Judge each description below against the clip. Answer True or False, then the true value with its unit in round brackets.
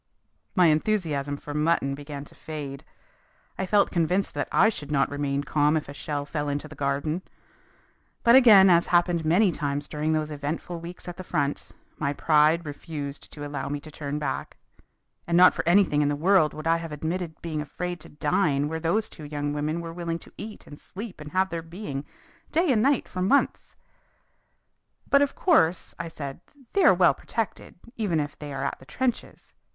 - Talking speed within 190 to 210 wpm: True (195 wpm)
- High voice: False (155 Hz)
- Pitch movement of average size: True (3.6 semitones)